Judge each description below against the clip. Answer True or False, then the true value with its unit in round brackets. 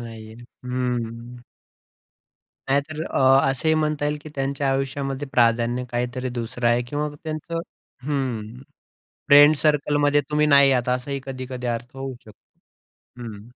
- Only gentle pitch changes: False (3.1 semitones)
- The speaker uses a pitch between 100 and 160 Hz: True (135 Hz)